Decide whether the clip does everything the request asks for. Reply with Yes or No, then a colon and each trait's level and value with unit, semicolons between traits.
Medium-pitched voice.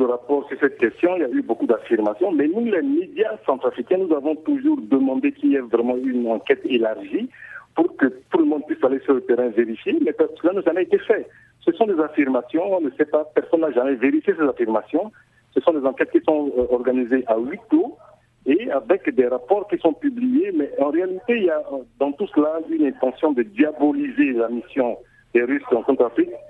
Yes: medium, 160 Hz